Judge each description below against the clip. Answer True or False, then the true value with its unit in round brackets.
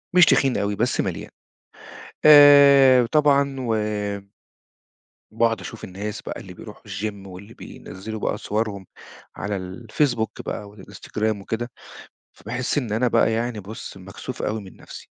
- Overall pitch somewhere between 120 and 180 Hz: False (110 Hz)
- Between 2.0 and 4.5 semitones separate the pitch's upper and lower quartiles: True (4.0 semitones)